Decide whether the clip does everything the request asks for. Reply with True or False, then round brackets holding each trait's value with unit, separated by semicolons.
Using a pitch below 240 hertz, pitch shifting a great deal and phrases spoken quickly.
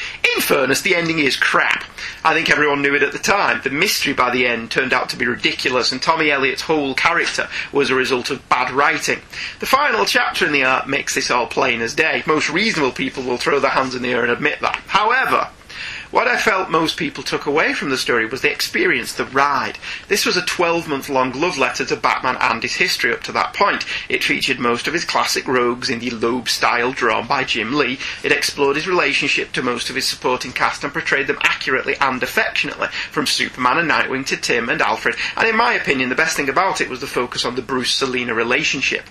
False (135 Hz; 3.9 semitones; 225 wpm)